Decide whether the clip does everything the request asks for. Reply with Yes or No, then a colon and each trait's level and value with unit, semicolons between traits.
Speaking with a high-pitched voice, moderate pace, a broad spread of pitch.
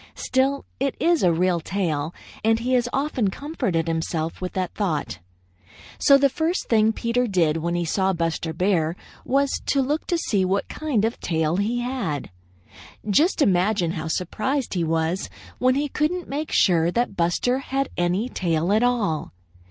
Yes: high, 200 Hz; average, 170 wpm; wide, 7.4 semitones